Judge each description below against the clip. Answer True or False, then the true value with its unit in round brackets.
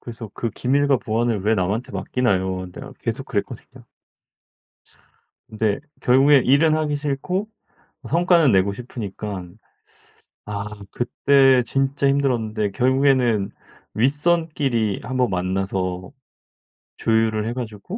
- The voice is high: False (120 Hz)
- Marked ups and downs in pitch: False (4.9 semitones)